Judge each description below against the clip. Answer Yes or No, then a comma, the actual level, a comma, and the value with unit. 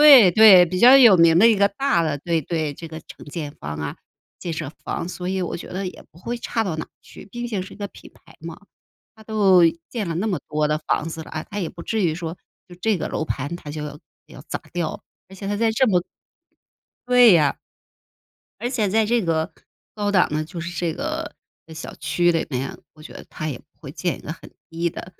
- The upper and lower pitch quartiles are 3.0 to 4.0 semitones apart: No, average, 4.6 semitones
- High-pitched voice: No, medium, 175 Hz